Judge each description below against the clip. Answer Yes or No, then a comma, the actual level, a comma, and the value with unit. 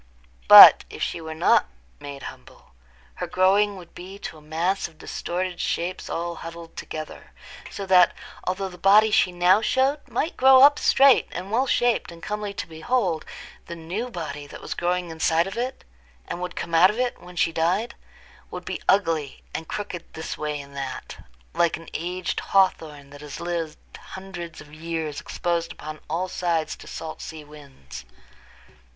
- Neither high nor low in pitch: Yes, medium, 175 Hz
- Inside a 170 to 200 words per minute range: Yes, average, 175 wpm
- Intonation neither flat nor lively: Yes, average, 3.4 semitones